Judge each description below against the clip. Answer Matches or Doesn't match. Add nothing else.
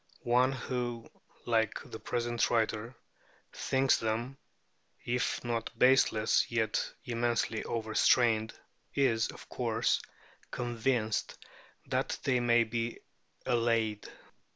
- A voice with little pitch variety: Matches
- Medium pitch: Doesn't match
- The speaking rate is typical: Doesn't match